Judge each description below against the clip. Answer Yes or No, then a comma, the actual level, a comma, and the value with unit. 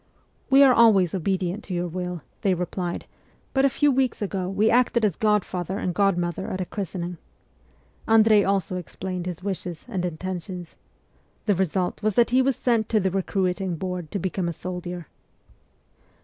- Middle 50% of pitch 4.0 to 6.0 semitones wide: No, average, 3.1 semitones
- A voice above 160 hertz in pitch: Yes, high, 190 Hz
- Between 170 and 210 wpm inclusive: Yes, average, 175 wpm